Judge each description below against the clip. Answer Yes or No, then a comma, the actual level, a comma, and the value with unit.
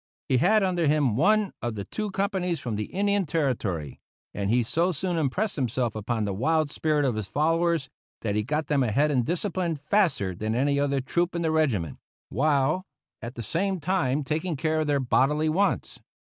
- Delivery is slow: No, average, 190 wpm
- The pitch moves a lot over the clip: Yes, wide, 6.0 semitones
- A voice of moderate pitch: Yes, medium, 150 Hz